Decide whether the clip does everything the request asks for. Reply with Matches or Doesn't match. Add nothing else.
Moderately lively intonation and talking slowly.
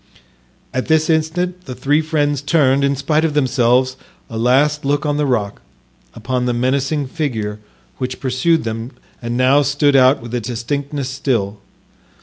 Doesn't match